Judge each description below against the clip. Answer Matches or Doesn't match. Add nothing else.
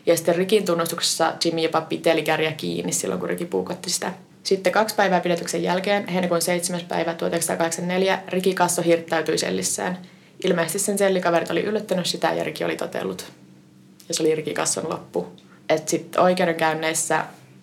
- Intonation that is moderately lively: Doesn't match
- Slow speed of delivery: Doesn't match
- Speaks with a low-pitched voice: Doesn't match